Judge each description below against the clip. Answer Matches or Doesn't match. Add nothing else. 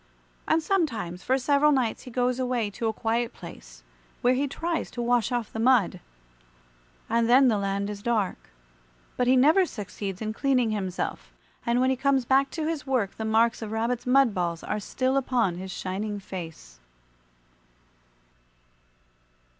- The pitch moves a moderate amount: Matches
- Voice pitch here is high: Matches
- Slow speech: Doesn't match